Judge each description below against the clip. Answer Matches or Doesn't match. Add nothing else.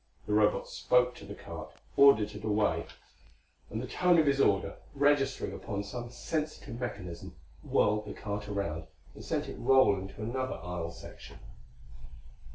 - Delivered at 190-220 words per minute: Doesn't match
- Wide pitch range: Doesn't match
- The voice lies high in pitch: Doesn't match